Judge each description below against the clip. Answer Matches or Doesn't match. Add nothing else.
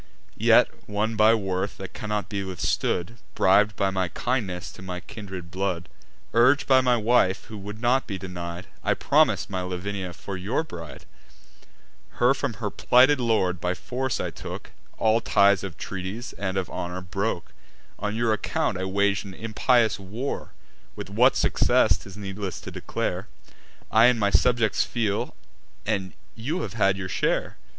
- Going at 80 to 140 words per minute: Doesn't match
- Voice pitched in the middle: Doesn't match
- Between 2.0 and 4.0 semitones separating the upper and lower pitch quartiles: Matches